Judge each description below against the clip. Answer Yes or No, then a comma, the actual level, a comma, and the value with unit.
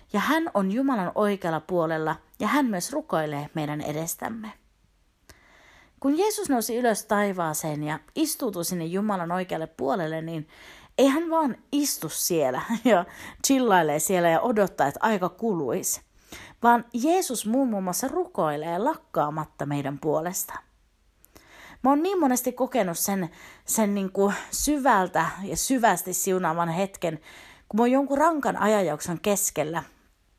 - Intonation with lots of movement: Yes, wide, 7.5 semitones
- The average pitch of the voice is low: No, high, 200 Hz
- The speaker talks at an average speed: Yes, average, 130 wpm